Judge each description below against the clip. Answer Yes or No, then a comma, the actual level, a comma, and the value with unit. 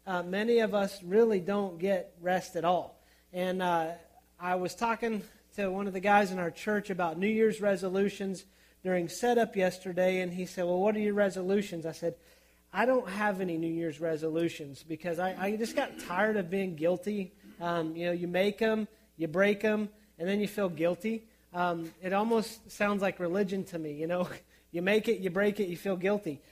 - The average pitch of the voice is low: No, high, 190 Hz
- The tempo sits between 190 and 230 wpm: Yes, average, 200 wpm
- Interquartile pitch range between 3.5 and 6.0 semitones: No, average, 2.9 semitones